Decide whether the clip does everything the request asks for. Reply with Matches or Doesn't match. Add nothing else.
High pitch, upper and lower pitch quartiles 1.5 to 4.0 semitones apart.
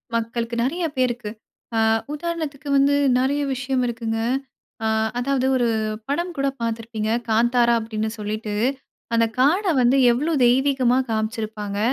Matches